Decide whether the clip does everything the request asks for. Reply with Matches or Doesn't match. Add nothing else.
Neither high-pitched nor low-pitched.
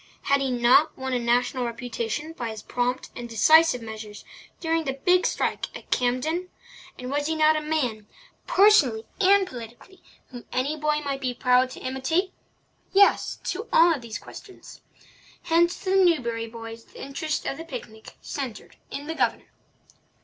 Doesn't match